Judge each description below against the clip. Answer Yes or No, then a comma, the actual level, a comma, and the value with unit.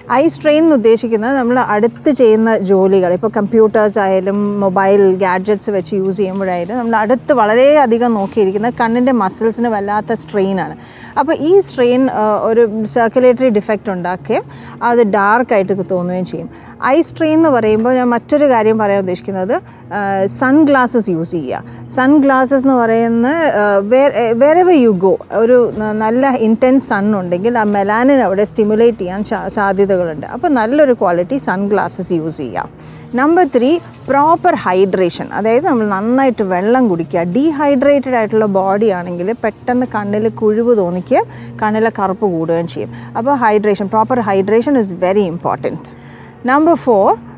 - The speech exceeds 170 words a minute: No, fast, 125 wpm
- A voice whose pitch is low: No, high, 220 Hz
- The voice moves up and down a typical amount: Yes, average, 4.5 semitones